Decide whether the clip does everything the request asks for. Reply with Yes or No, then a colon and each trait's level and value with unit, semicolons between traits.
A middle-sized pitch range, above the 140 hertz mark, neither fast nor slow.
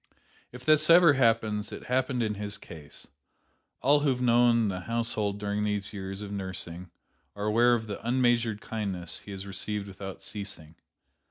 No: average, 3.4 semitones; low, 105 Hz; average, 165 wpm